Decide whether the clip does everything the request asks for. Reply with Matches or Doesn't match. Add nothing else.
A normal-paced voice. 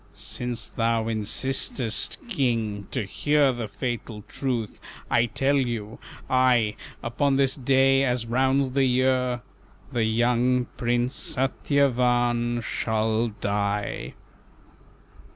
Doesn't match